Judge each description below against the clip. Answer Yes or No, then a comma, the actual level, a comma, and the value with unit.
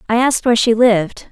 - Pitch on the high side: Yes, high, 230 Hz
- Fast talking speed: Yes, fast, 230 wpm